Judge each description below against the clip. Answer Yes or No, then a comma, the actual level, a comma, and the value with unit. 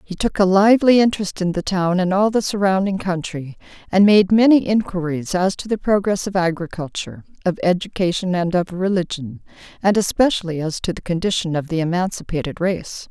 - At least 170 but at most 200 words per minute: Yes, average, 175 wpm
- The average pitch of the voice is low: No, medium, 185 Hz